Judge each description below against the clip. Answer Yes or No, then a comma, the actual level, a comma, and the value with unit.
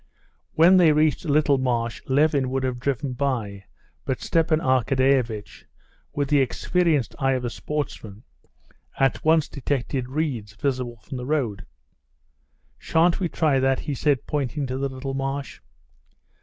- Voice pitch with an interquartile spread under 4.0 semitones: Yes, average, 2.9 semitones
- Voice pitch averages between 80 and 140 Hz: Yes, low, 135 Hz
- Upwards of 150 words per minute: No, average, 145 wpm